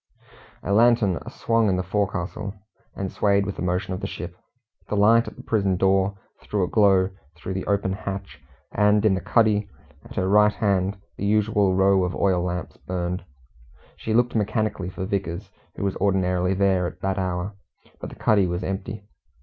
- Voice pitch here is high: No, very low, 95 Hz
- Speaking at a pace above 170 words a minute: Yes, average, 180 wpm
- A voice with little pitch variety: Yes, narrow, 2.0 semitones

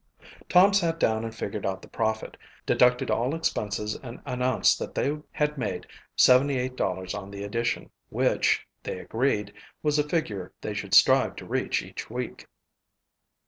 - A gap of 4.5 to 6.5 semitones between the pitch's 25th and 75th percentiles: Yes, average, 5.2 semitones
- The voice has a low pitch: Yes, low, 120 Hz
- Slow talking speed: No, average, 150 wpm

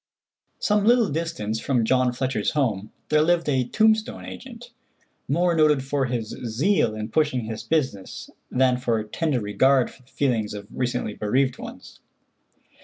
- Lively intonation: Yes, wide, 5.8 semitones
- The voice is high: No, low, 130 Hz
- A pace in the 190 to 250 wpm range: No, average, 150 wpm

